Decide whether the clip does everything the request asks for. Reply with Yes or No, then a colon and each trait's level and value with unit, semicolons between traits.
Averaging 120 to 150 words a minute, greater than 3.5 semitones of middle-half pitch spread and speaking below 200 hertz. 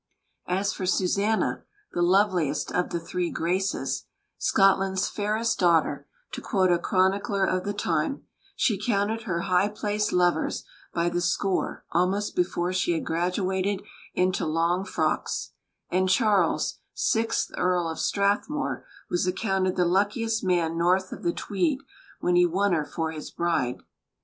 No: average, 145 wpm; narrow, 2.6 semitones; medium, 185 Hz